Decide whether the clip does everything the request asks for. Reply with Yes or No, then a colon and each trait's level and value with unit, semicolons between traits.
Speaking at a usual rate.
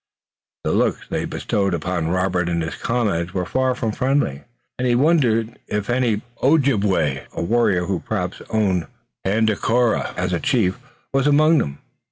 Yes: average, 155 wpm